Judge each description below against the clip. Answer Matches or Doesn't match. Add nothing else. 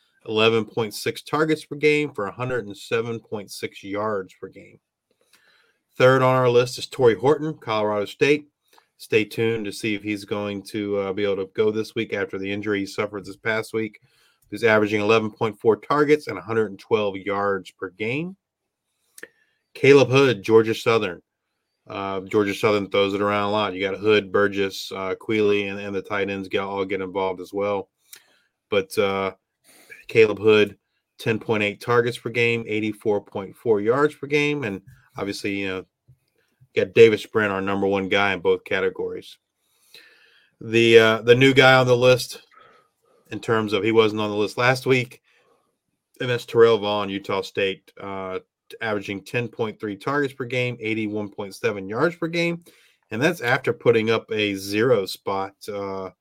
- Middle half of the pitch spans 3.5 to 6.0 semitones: Matches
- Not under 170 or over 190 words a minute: Doesn't match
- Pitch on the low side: Matches